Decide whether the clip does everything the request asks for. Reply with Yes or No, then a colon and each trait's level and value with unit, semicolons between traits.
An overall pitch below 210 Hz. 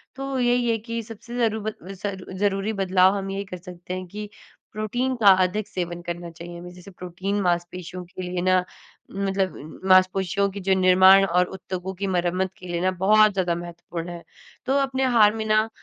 Yes: high, 190 Hz